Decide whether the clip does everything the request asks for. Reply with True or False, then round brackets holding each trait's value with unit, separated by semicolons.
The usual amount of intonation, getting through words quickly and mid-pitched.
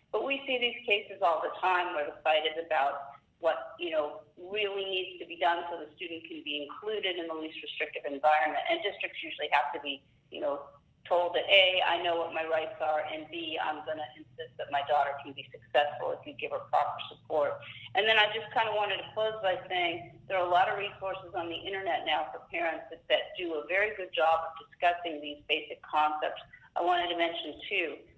True (3.6 semitones; 230 wpm; 165 Hz)